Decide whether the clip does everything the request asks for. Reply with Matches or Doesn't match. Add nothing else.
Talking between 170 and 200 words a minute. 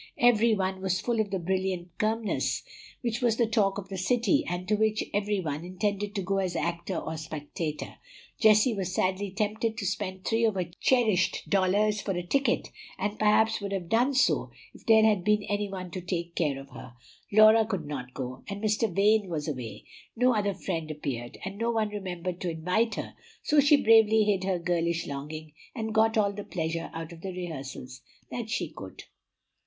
Matches